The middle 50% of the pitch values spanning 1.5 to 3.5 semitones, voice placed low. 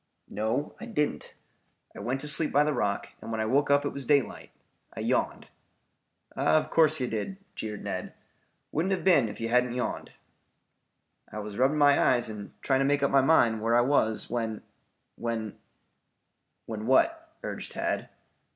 No: average, 4.7 semitones; low, 130 Hz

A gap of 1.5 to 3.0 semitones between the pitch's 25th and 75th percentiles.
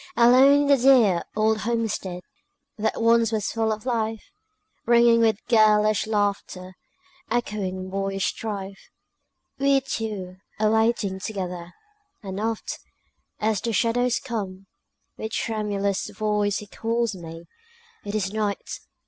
Yes: average, 2.7 semitones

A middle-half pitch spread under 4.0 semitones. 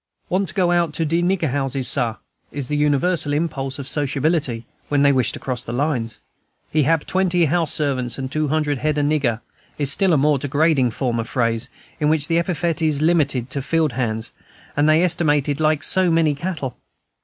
Yes: average, 3.4 semitones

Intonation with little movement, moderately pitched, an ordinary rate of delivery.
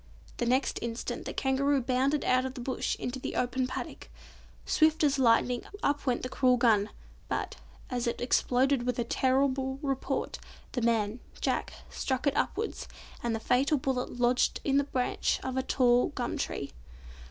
No: narrow, 1.7 semitones; very high, 255 Hz; average, 170 wpm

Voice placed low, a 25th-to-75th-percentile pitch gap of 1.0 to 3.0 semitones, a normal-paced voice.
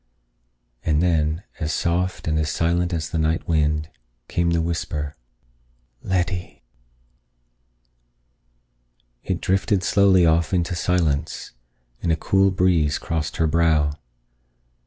No: very low, 85 Hz; narrow, 2.5 semitones; slow, 115 wpm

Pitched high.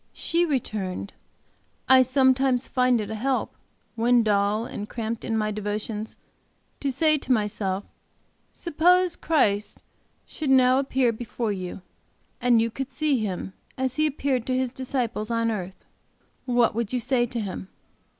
Yes: high, 240 Hz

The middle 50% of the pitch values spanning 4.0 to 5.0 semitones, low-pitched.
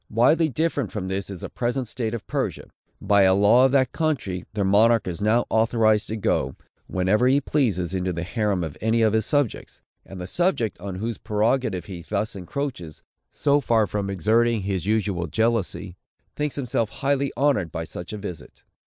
Yes: average, 4.3 semitones; low, 110 Hz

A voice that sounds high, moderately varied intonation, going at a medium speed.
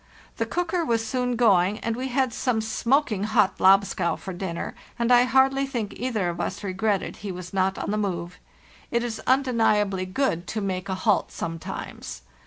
Yes: high, 215 Hz; average, 4.7 semitones; average, 180 wpm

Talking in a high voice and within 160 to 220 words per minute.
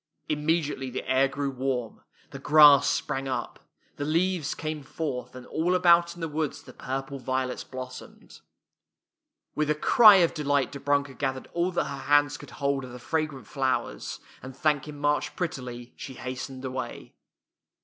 No: medium, 140 Hz; average, 170 wpm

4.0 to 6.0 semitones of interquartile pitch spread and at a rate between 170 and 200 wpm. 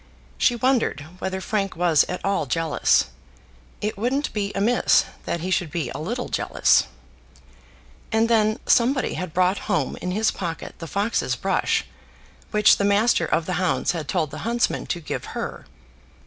No: average, 4.6 semitones; average, 160 wpm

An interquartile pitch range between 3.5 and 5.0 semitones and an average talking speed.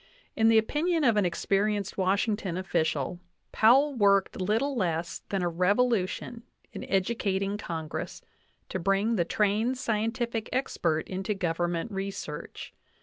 No: average, 3.8 semitones; slow, 130 wpm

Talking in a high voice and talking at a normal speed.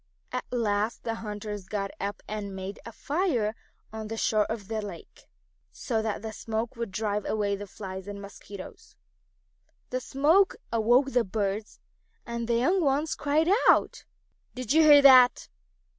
Yes: high, 220 Hz; average, 160 wpm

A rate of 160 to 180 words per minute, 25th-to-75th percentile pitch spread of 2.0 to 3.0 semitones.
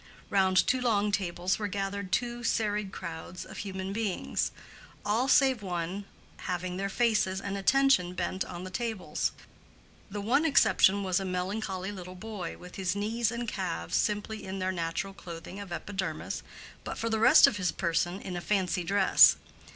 Yes: average, 165 wpm; average, 2.7 semitones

